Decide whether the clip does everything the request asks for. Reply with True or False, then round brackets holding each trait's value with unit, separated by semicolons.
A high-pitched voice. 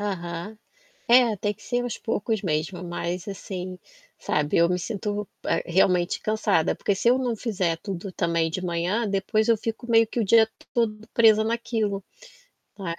True (205 Hz)